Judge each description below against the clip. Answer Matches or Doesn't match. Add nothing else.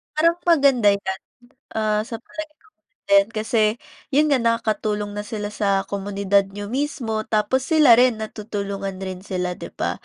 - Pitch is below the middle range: Doesn't match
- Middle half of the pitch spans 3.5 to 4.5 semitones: Matches